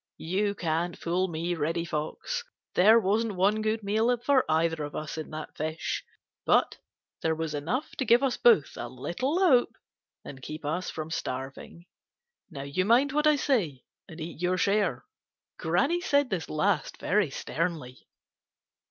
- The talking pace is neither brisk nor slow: Yes, average, 160 wpm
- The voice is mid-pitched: Yes, medium, 180 Hz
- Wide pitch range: Yes, wide, 6.2 semitones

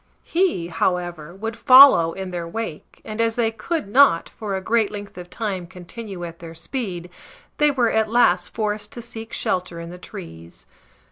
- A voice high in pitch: Yes, high, 200 Hz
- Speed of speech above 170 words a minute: Yes, average, 180 wpm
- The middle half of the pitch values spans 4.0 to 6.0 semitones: Yes, average, 4.6 semitones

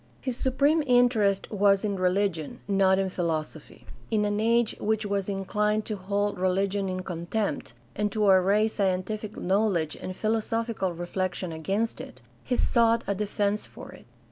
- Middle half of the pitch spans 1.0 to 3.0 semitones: Yes, narrow, 2.6 semitones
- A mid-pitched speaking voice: No, high, 200 Hz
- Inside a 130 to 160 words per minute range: Yes, average, 150 wpm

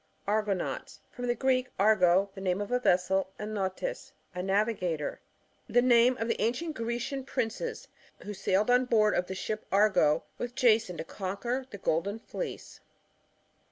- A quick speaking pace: No, average, 160 wpm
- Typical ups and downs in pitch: Yes, average, 4.2 semitones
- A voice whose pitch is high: Yes, high, 215 Hz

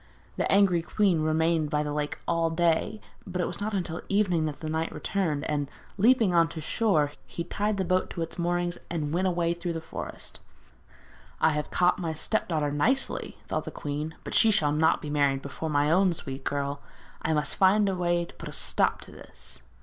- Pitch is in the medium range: Yes, medium, 165 Hz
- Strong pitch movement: No, average, 3.5 semitones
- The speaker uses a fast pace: Yes, fast, 210 wpm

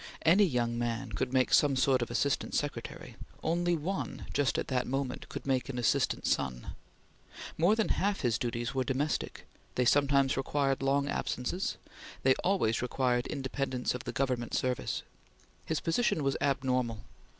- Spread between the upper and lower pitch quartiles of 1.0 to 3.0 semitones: Yes, average, 2.7 semitones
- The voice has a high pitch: No, low, 135 Hz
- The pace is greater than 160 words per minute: No, average, 155 wpm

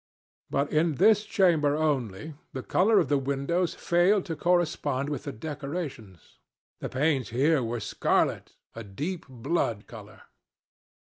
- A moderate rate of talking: No, slow, 130 wpm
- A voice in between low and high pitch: Yes, medium, 145 Hz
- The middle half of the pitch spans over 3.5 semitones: Yes, average, 5.1 semitones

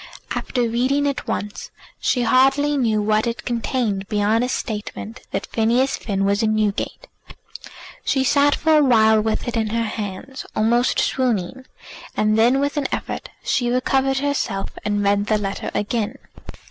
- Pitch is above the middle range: Yes, high, 230 Hz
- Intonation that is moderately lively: Yes, average, 3.8 semitones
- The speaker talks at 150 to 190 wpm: Yes, average, 160 wpm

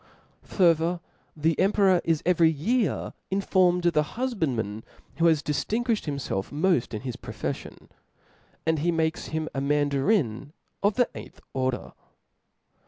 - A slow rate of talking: Yes, slow, 130 wpm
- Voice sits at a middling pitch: Yes, medium, 160 Hz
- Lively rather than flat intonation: No, average, 4.8 semitones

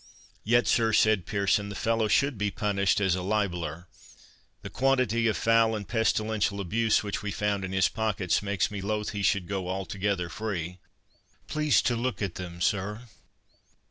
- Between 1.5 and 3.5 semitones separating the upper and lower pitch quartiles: Yes, narrow, 2.6 semitones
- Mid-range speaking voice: No, low, 105 Hz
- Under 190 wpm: Yes, average, 165 wpm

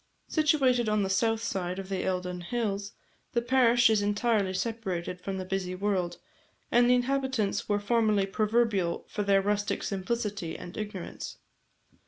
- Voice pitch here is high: Yes, high, 205 Hz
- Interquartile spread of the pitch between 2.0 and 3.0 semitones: No, average, 3.6 semitones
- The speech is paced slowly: No, average, 150 wpm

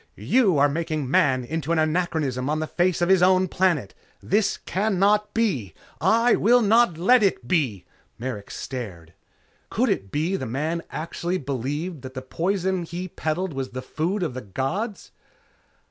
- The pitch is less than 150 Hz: No, medium, 165 Hz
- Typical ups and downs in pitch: No, wide, 6.1 semitones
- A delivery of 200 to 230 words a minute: No, average, 165 wpm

